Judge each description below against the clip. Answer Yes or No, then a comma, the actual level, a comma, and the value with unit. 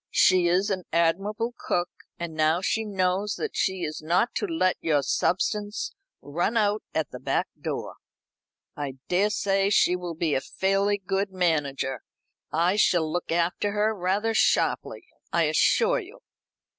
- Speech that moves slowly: No, average, 150 wpm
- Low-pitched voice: No, medium, 185 Hz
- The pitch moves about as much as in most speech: Yes, average, 3.4 semitones